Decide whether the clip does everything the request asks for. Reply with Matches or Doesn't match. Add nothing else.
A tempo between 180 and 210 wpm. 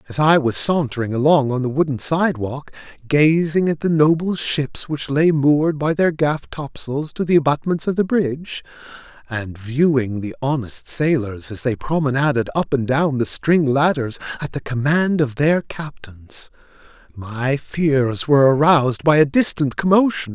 Doesn't match